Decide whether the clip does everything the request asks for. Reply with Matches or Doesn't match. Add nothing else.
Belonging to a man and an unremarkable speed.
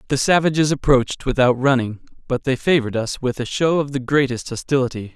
Matches